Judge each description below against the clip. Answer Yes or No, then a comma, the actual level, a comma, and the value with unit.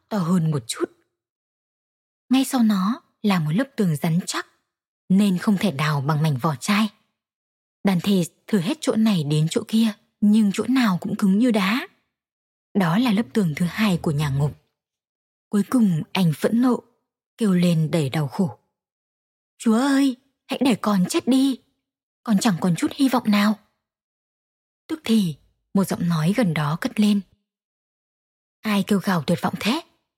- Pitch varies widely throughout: No, average, 4.9 semitones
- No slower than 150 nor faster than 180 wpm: Yes, average, 170 wpm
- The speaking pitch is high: Yes, high, 205 Hz